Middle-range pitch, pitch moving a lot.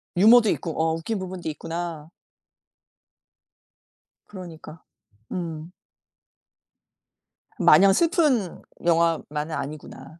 No: medium, 170 Hz; average, 3.1 semitones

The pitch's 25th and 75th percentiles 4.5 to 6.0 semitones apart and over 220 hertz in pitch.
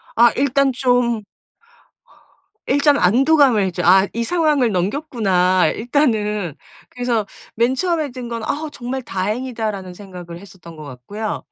Yes: wide, 5.6 semitones; high, 230 Hz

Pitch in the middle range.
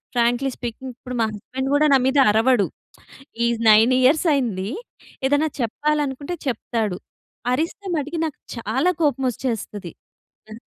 No: very high, 255 Hz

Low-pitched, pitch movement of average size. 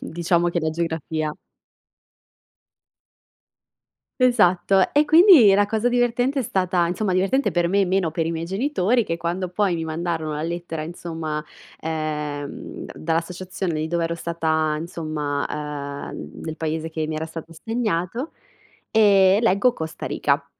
No: medium, 170 Hz; average, 3.6 semitones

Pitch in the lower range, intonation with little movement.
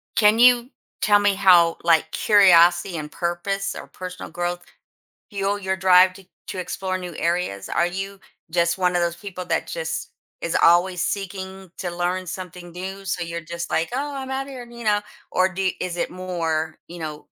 No: medium, 185 Hz; narrow, 2.2 semitones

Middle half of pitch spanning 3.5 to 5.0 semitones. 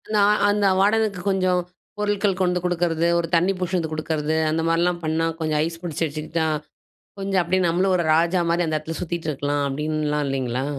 No: average, 3.0 semitones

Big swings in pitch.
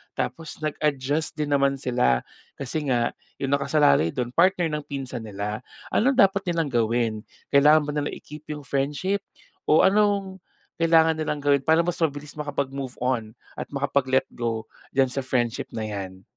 No: average, 4.1 semitones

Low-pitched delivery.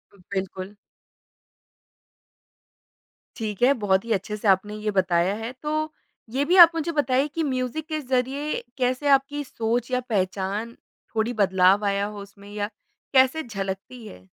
No: high, 225 Hz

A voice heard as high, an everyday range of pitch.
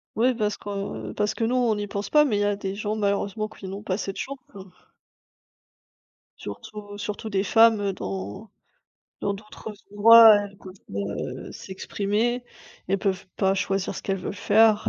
No: high, 205 Hz; narrow, 1.8 semitones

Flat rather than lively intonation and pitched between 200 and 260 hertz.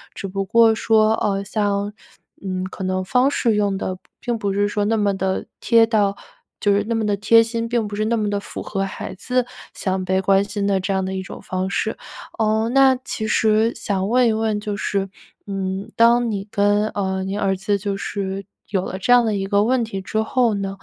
Yes: narrow, 2.3 semitones; high, 205 Hz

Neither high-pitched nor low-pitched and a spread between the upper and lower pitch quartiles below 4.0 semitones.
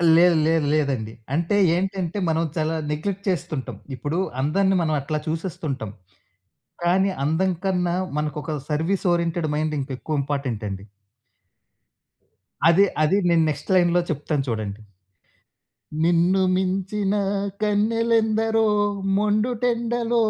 No: medium, 170 Hz; average, 4.6 semitones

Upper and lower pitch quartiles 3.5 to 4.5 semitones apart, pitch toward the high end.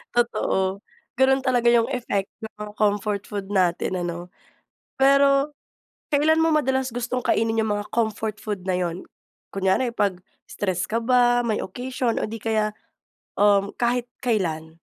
Yes: average, 3.9 semitones; high, 220 Hz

